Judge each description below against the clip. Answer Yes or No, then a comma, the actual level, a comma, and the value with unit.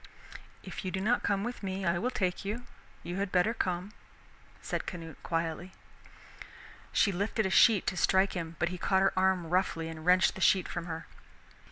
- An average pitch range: No, narrow, 2.2 semitones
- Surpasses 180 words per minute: Yes, average, 190 wpm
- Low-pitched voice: No, medium, 185 Hz